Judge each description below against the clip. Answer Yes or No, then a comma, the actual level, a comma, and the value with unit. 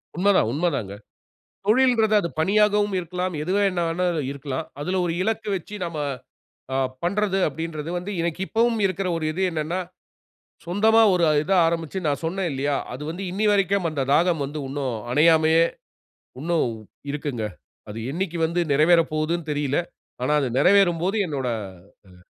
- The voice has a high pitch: No, medium, 170 Hz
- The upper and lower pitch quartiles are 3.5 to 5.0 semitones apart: Yes, average, 4.2 semitones